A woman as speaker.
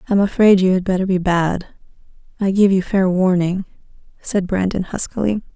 Yes: female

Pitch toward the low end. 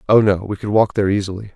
Yes: low, 100 Hz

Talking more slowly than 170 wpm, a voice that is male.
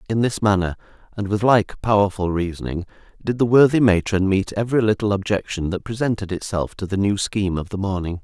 No: average, 190 wpm; male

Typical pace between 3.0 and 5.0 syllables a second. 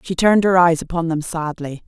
No: 5.7 syllables/s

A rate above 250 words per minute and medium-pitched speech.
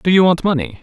Yes: fast, 290 wpm; medium, 175 Hz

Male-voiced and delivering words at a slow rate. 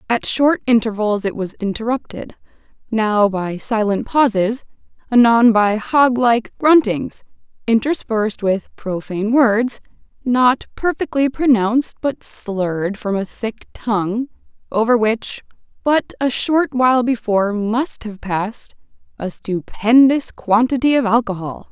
No: female; slow, 115 wpm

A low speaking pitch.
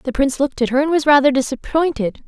No: very high, 275 Hz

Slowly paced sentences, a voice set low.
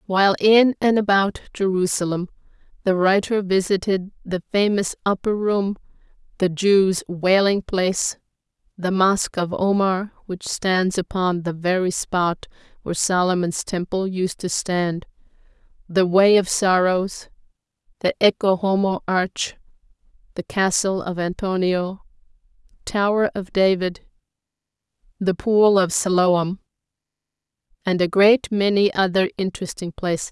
No: slow, 115 wpm; high, 190 Hz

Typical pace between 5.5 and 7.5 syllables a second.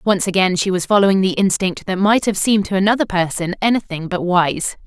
Yes: 5.8 syllables/s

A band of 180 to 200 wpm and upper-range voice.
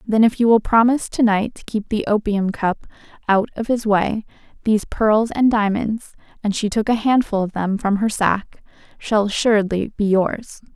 Yes: average, 190 wpm; high, 215 Hz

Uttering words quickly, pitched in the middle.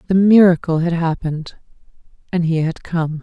No: average, 150 wpm; medium, 170 Hz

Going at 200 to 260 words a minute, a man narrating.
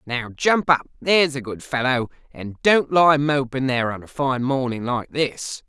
No: average, 190 wpm; male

